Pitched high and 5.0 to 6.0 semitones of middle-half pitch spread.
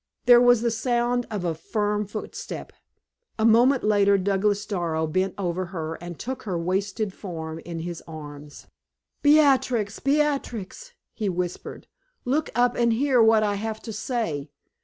Yes: high, 210 Hz; average, 5.3 semitones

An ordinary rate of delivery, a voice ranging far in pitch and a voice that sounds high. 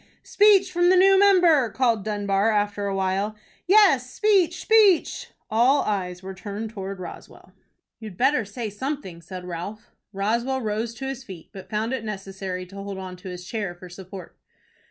Yes: average, 170 wpm; wide, 5.7 semitones; high, 215 Hz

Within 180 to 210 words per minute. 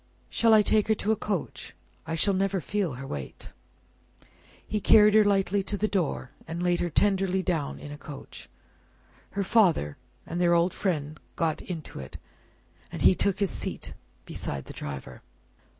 No: average, 170 wpm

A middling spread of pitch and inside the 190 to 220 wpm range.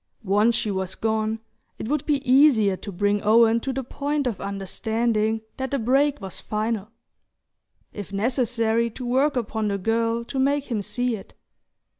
No: average, 3.5 semitones; average, 165 wpm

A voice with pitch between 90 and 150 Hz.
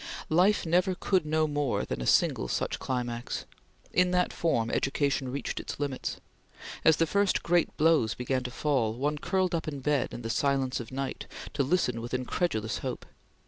Yes: medium, 140 Hz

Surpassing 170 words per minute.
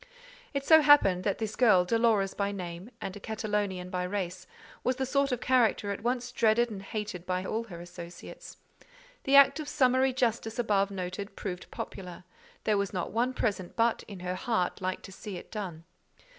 Yes: average, 185 wpm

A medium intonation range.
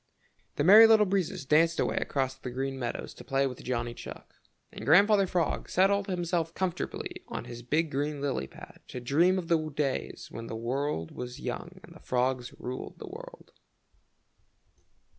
No: wide, 6.2 semitones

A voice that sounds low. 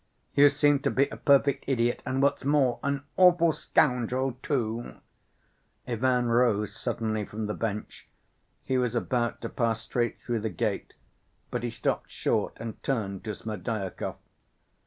Yes: low, 120 Hz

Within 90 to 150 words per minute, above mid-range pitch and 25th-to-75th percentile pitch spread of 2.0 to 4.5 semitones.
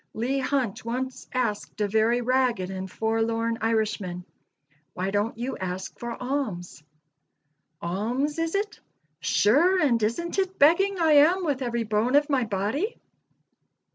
No: average, 140 wpm; high, 235 Hz; average, 5.3 semitones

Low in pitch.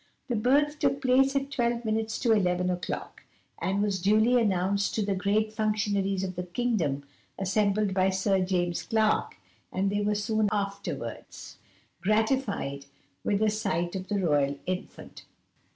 No: high, 205 Hz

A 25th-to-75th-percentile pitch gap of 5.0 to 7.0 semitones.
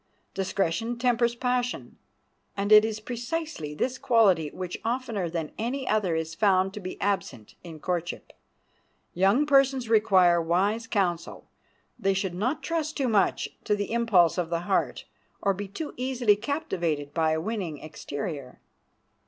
Yes: wide, 5.6 semitones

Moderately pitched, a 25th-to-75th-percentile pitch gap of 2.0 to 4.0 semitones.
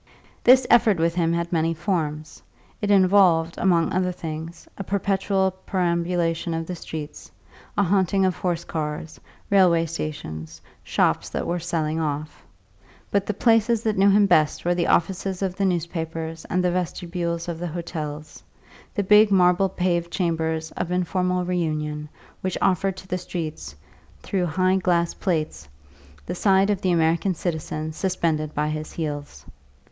Yes: medium, 175 Hz; average, 2.8 semitones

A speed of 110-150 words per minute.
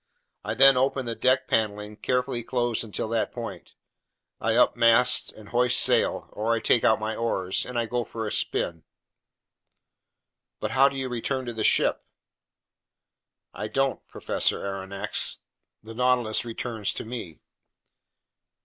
Yes: average, 140 wpm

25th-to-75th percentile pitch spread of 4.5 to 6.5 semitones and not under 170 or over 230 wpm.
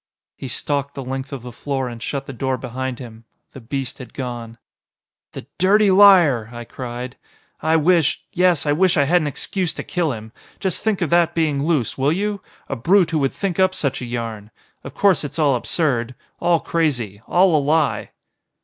Yes: wide, 5.5 semitones; average, 195 wpm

